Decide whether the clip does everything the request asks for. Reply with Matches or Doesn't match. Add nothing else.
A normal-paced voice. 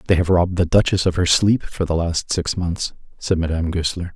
Doesn't match